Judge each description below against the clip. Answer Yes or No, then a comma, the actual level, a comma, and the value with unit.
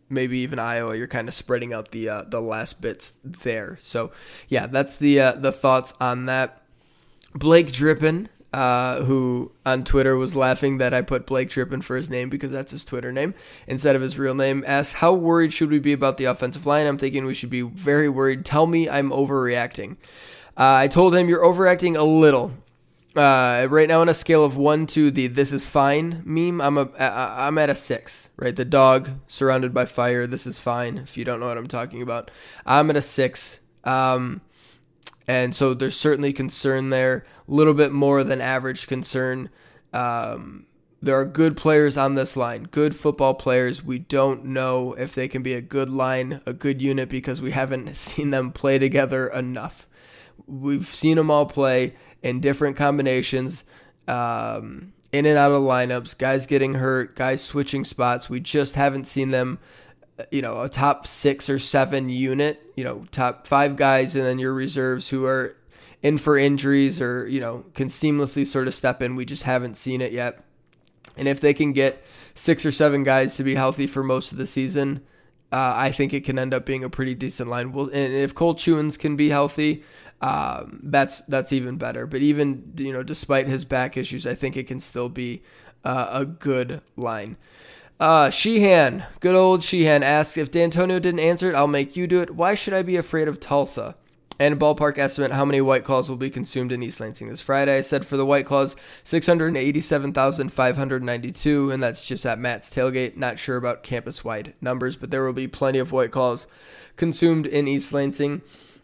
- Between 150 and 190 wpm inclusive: No, average, 200 wpm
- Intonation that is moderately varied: No, narrow, 2.2 semitones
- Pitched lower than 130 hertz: No, low, 135 Hz